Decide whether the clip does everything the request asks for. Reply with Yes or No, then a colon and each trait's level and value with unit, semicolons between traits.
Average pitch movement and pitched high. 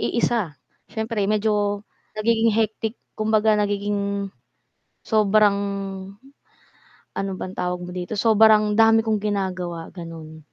No: narrow, 2.0 semitones; high, 210 Hz